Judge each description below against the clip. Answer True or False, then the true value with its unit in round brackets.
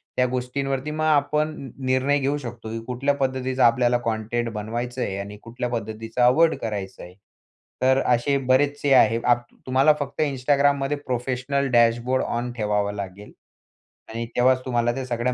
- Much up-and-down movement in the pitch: False (2.7 semitones)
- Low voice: True (125 Hz)